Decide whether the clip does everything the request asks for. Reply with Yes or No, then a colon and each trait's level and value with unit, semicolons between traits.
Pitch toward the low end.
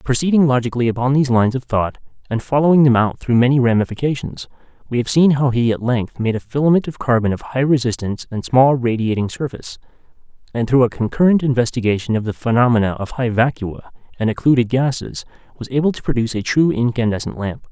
Yes: low, 120 Hz